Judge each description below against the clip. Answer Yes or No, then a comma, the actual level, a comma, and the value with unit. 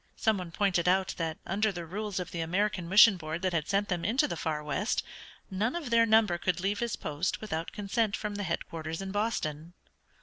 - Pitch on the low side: No, high, 190 Hz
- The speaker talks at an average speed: No, fast, 210 wpm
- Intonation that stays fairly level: No, average, 3.9 semitones